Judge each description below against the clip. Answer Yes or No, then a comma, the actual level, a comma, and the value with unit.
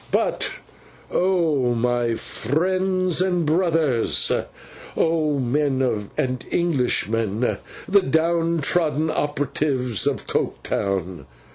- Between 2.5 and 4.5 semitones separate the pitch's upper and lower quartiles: No, wide, 5.5 semitones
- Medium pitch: Yes, medium, 145 Hz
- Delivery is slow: Yes, slow, 85 wpm